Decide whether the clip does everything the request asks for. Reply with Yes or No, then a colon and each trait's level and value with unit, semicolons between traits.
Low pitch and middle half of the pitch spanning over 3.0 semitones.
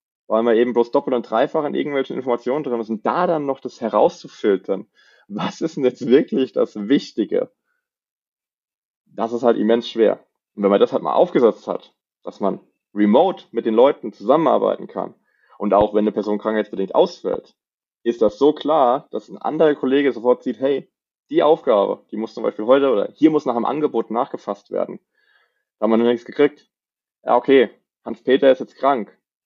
Yes: low, 120 Hz; average, 3.7 semitones